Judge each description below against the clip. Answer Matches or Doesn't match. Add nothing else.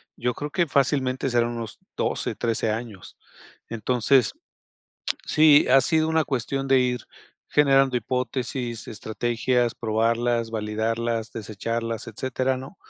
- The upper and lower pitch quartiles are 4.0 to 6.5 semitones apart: Doesn't match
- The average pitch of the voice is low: Matches